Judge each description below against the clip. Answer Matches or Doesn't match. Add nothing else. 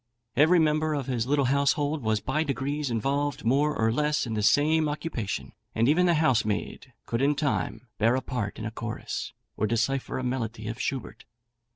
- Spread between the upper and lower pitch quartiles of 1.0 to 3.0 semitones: Doesn't match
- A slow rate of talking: Doesn't match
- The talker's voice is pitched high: Doesn't match